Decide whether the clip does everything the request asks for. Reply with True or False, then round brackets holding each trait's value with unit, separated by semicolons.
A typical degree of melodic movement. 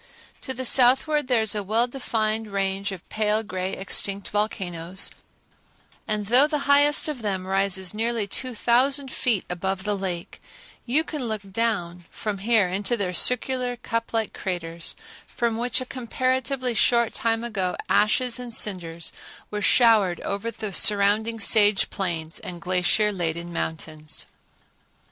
True (4.0 semitones)